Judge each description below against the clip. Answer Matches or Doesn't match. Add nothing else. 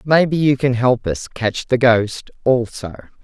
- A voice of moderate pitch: Doesn't match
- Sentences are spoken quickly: Doesn't match